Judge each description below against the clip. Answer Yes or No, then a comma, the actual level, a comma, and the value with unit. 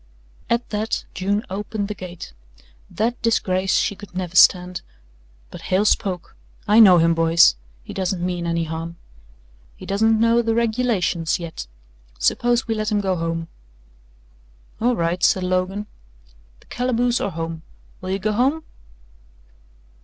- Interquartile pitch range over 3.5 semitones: Yes, average, 4.3 semitones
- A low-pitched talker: No, high, 190 Hz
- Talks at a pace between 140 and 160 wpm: Yes, average, 145 wpm